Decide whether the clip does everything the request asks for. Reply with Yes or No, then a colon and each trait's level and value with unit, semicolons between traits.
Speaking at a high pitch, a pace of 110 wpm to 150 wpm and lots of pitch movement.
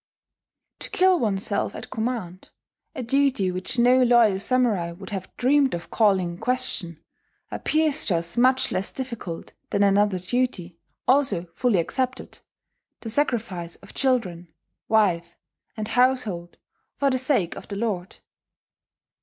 Yes: high, 220 Hz; slow, 135 wpm; wide, 5.7 semitones